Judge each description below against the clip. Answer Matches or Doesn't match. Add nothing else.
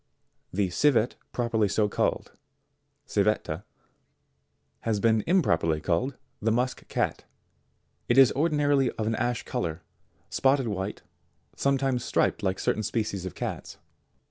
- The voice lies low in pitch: Matches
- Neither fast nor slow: Doesn't match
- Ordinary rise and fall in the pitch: Matches